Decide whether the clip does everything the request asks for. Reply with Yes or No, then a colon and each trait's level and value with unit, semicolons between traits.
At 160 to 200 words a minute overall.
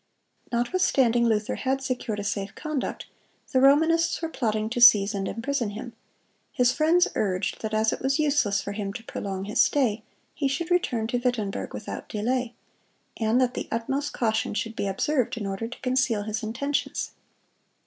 Yes: average, 170 wpm